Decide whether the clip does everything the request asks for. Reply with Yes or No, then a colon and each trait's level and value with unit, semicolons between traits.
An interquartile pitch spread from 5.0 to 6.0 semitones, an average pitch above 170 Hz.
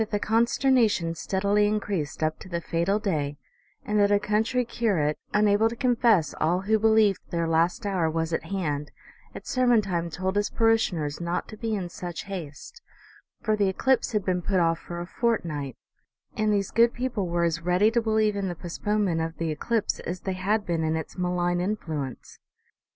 No: average, 4.3 semitones; high, 190 Hz